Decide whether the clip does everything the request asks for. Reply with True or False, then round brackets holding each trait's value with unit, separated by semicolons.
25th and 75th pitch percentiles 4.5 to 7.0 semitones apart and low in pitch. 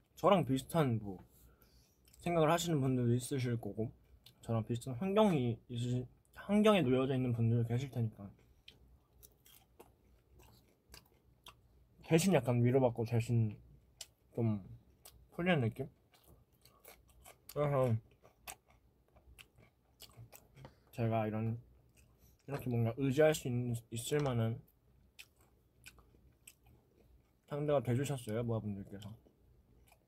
False (4.0 semitones; 120 Hz)